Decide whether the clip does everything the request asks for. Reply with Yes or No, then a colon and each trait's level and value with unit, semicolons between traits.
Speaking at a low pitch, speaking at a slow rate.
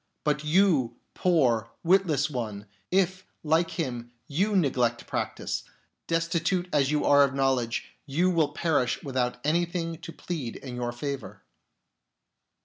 No: medium, 150 Hz; slow, 130 wpm